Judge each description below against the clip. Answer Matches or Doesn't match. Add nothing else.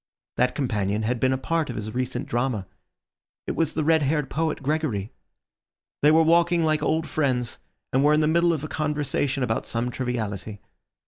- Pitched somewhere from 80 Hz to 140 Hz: Matches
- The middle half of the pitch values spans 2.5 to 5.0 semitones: Matches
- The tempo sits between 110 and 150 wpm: Doesn't match